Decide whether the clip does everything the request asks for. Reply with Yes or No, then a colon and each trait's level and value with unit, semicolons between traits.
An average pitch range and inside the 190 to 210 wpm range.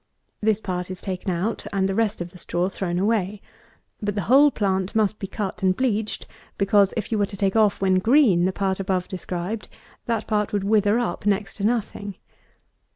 No: narrow, 2.3 semitones; average, 200 wpm